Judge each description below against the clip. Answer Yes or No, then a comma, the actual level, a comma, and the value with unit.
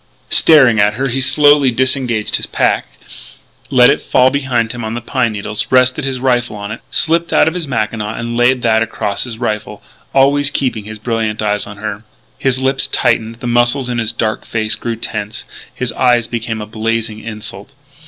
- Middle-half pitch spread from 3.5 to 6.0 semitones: No, average, 3.1 semitones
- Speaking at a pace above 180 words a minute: Yes, average, 190 wpm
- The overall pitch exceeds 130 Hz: No, low, 120 Hz